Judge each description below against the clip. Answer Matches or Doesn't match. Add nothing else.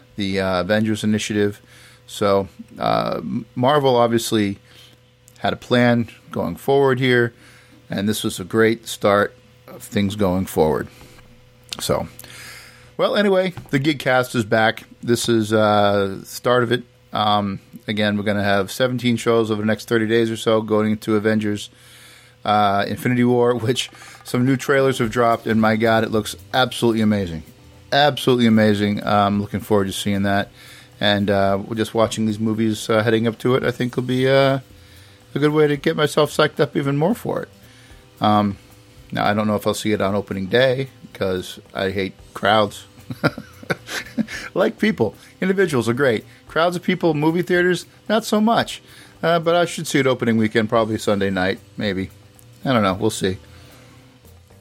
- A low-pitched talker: Matches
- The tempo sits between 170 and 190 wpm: Matches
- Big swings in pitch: Doesn't match